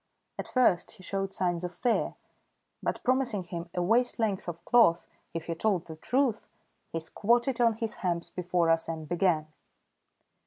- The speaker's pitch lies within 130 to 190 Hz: Yes, medium, 185 Hz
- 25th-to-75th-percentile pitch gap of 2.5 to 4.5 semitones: No, average, 5.1 semitones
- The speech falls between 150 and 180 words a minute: Yes, average, 165 wpm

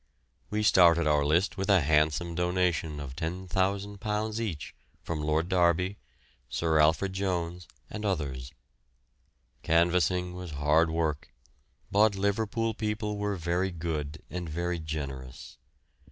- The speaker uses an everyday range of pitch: Yes, average, 3.8 semitones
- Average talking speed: No, slow, 120 wpm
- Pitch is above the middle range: No, very low, 85 Hz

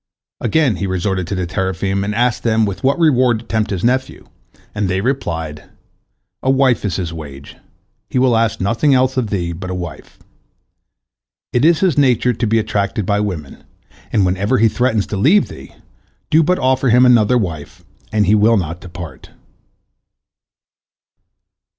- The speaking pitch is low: Yes, low, 105 Hz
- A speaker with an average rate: Yes, average, 170 wpm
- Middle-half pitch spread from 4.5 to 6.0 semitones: Yes, average, 5.2 semitones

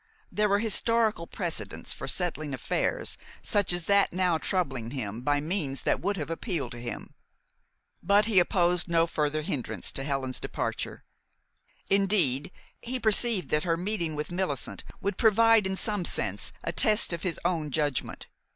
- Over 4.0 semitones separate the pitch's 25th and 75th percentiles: Yes, wide, 5.4 semitones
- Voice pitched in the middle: Yes, medium, 175 Hz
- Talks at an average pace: Yes, average, 160 wpm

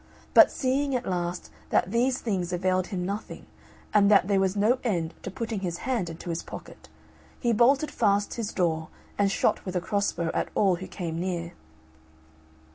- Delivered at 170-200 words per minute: Yes, average, 185 wpm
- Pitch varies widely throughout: No, average, 4.1 semitones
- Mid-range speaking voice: No, high, 195 Hz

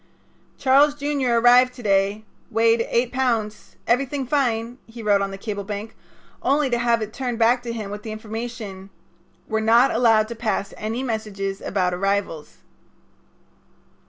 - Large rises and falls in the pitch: No, average, 2.9 semitones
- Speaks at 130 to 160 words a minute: Yes, average, 155 wpm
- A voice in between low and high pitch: No, high, 225 Hz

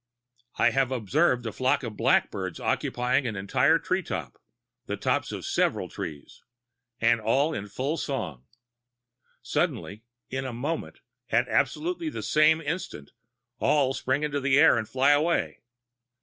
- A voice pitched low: Yes, low, 130 Hz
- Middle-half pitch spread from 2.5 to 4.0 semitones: No, average, 4.5 semitones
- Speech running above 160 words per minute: No, average, 140 wpm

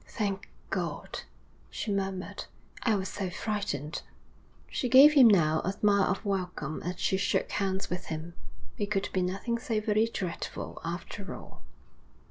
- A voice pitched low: No, high, 195 Hz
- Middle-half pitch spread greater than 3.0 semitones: No, average, 2.7 semitones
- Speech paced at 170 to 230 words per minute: No, average, 150 wpm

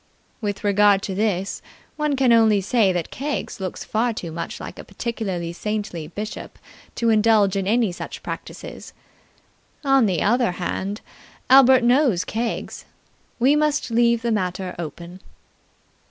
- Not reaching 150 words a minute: Yes, average, 140 wpm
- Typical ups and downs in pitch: Yes, average, 4.1 semitones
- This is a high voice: Yes, high, 215 Hz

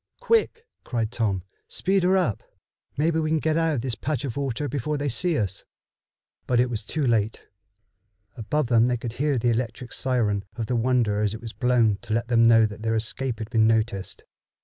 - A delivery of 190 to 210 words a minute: Yes, fast, 205 wpm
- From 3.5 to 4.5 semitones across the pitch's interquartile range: Yes, average, 4.2 semitones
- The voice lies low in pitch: Yes, low, 120 Hz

